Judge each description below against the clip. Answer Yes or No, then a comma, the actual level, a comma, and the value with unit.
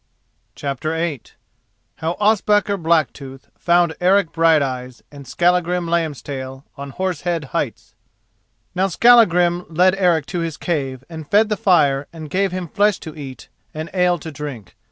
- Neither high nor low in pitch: Yes, medium, 165 Hz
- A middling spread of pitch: Yes, average, 3.9 semitones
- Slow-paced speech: No, average, 145 wpm